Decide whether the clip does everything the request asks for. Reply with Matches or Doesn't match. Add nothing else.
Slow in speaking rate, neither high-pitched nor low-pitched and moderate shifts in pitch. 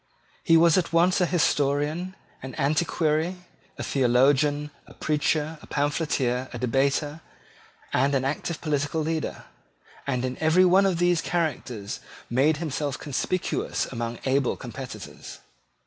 Matches